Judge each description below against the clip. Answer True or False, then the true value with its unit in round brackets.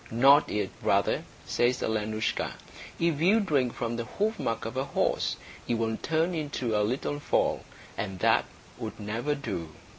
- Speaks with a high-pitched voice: False (120 Hz)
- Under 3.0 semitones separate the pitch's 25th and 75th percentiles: False (4.9 semitones)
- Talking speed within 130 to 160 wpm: True (155 wpm)